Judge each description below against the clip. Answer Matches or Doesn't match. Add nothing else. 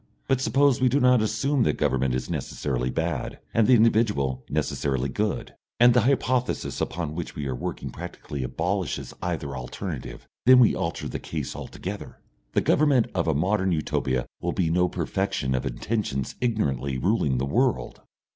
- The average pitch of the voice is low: Matches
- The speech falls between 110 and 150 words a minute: Doesn't match